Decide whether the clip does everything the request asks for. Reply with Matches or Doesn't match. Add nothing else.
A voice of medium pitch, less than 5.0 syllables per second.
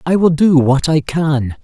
Matches